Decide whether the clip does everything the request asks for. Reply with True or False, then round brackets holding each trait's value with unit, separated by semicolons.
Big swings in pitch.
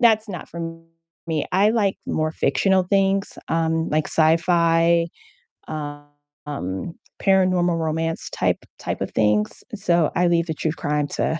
False (2.7 semitones)